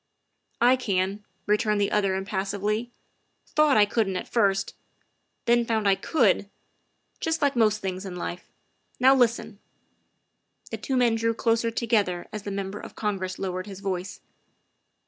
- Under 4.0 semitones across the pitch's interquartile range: Yes, average, 3.2 semitones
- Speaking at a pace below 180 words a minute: Yes, average, 165 wpm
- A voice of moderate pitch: No, high, 210 Hz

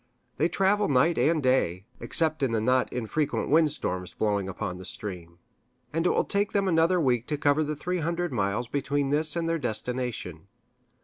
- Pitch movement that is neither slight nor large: No, wide, 6.5 semitones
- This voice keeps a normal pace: Yes, average, 180 wpm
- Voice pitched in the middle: Yes, medium, 145 Hz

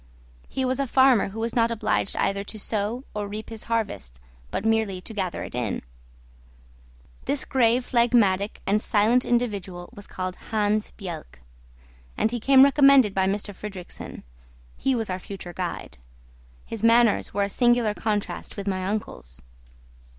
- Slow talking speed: No, average, 155 wpm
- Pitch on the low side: No, high, 210 Hz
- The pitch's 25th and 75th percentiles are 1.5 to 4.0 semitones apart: Yes, average, 3.4 semitones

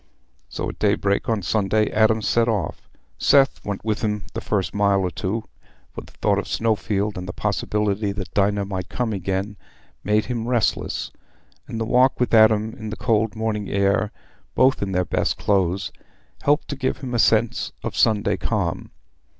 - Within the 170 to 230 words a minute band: Yes, average, 175 wpm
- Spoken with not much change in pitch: Yes, narrow, 2.2 semitones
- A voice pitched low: Yes, low, 105 Hz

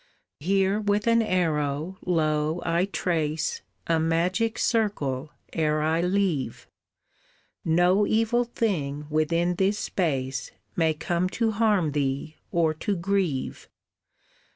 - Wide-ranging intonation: No, average, 4.5 semitones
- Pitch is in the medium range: Yes, medium, 170 Hz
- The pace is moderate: No, slow, 110 wpm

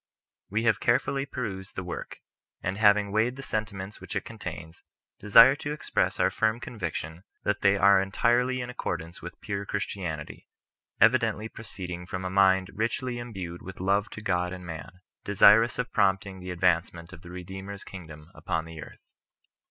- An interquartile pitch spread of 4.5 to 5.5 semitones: No, average, 3.5 semitones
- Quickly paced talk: No, average, 165 wpm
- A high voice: No, very low, 95 Hz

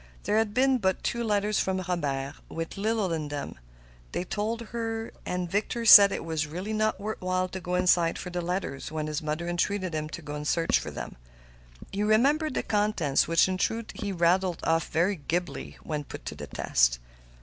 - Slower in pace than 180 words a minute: No, average, 195 wpm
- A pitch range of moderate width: Yes, average, 4.7 semitones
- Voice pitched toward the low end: No, medium, 180 Hz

